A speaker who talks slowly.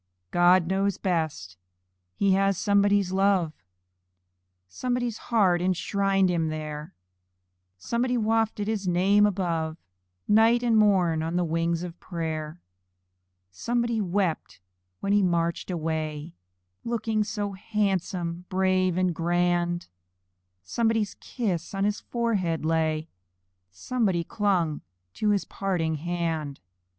Yes: slow, 110 wpm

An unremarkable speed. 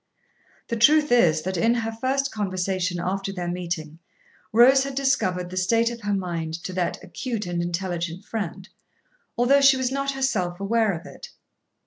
Yes: average, 165 wpm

